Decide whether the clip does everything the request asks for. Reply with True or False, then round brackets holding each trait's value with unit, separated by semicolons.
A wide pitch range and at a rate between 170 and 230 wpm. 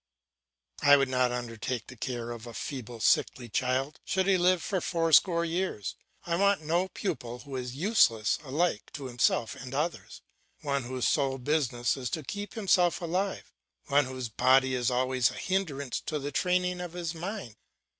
True (5.9 semitones; 175 wpm)